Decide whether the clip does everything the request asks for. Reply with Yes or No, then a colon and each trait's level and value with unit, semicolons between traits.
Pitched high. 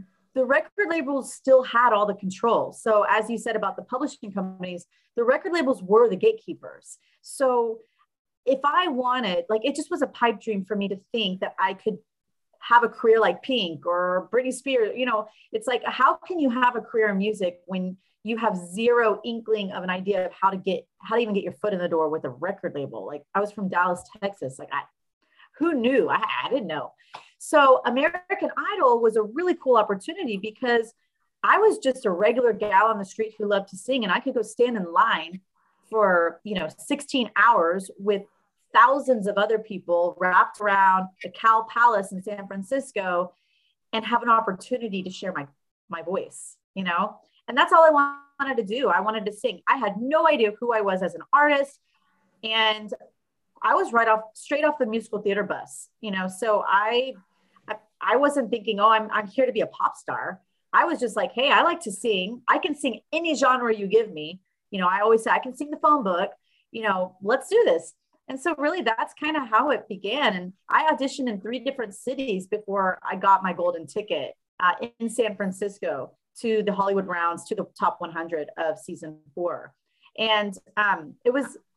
Yes: high, 220 Hz